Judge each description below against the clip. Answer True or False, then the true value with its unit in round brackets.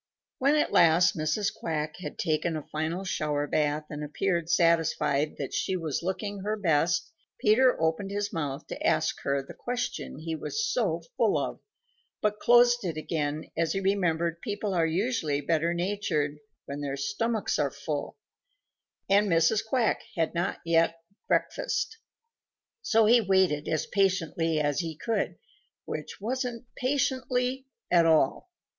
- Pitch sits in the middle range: True (170 Hz)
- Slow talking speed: False (150 wpm)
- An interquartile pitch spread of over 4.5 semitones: True (5.3 semitones)